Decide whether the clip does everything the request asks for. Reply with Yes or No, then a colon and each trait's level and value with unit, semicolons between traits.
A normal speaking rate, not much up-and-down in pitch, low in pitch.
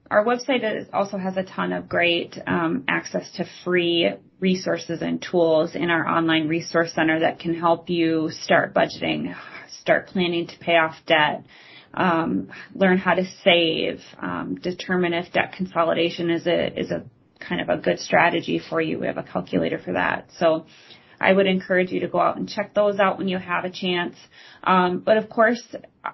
No: average, 185 wpm; narrow, 2.2 semitones; medium, 175 Hz